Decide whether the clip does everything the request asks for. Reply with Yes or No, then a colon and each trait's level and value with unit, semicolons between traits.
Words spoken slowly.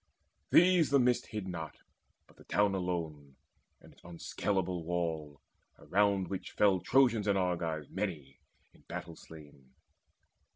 Yes: slow, 130 wpm